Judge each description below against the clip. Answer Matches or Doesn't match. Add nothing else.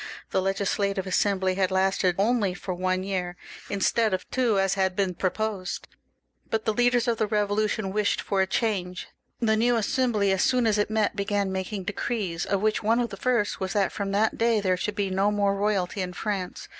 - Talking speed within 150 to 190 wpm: Doesn't match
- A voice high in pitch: Matches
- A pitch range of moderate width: Doesn't match